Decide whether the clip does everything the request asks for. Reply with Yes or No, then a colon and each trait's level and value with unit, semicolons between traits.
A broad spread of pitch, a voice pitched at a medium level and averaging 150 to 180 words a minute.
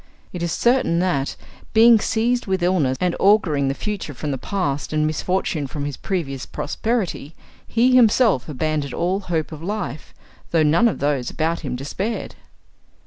Yes: wide, 6.0 semitones; medium, 170 Hz; average, 160 wpm